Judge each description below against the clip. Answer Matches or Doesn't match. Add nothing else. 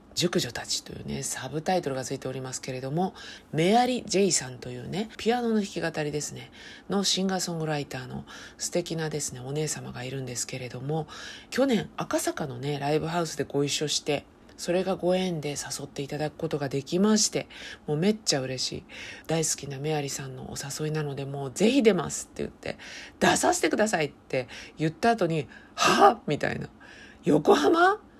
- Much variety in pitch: Doesn't match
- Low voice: Doesn't match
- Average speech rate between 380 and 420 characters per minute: Matches